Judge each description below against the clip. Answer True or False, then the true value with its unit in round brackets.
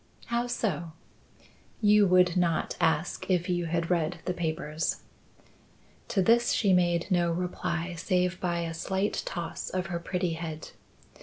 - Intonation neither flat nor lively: False (1.7 semitones)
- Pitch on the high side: False (175 Hz)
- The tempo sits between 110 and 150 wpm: True (145 wpm)